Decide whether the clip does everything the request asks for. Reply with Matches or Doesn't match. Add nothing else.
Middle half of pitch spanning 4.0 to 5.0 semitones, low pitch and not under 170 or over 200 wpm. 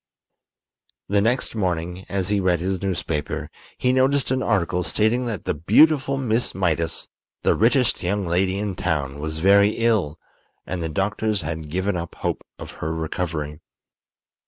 Doesn't match